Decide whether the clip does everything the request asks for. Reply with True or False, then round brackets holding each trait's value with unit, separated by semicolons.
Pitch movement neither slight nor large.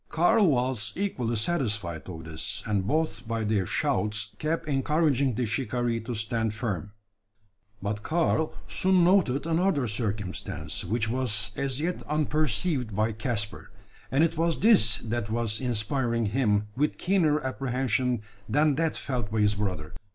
False (6.0 semitones)